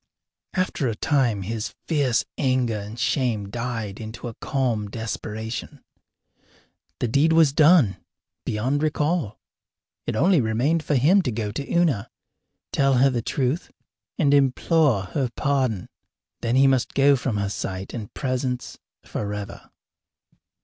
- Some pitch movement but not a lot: Yes, average, 4.5 semitones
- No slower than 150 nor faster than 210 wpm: No, slow, 135 wpm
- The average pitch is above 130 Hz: No, low, 125 Hz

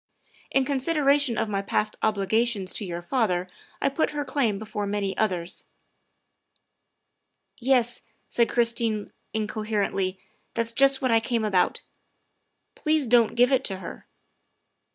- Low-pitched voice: No, high, 225 Hz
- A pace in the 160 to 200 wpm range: No, average, 145 wpm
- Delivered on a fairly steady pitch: No, average, 4.2 semitones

